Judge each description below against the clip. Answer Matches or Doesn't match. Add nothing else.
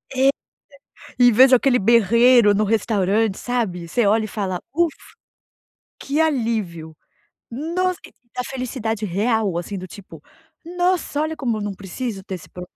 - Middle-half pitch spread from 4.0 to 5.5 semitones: Matches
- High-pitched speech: Matches